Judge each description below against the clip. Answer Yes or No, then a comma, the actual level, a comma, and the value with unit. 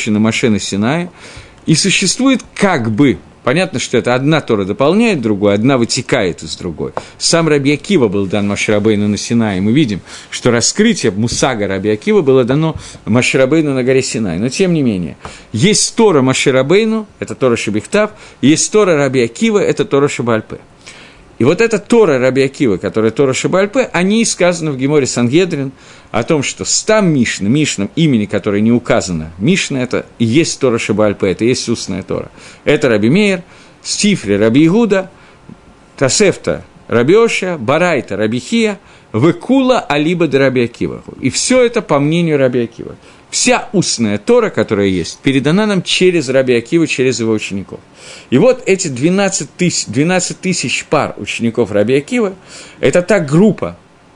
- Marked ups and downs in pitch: Yes, wide, 8.1 semitones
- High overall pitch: No, medium, 140 Hz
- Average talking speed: Yes, average, 150 wpm